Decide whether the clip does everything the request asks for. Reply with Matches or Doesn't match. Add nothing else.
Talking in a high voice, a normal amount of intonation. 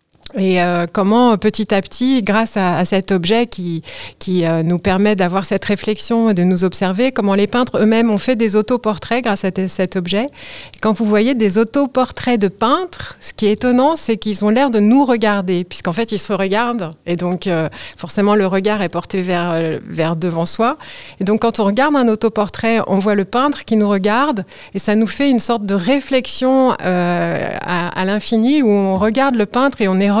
Matches